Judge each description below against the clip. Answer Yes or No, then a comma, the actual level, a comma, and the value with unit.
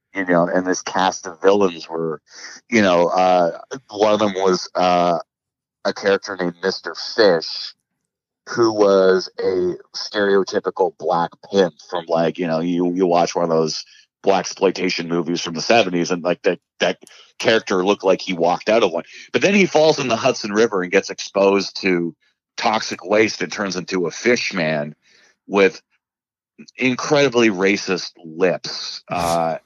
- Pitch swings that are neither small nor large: Yes, average, 3.3 semitones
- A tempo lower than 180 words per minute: Yes, average, 160 wpm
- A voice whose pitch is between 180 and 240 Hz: No, very low, 90 Hz